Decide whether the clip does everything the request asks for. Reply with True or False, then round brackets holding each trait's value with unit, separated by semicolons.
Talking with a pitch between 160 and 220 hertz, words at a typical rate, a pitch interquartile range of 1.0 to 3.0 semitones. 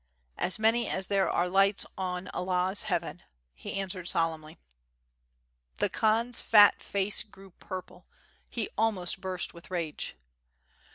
False (190 Hz; 130 wpm; 2.5 semitones)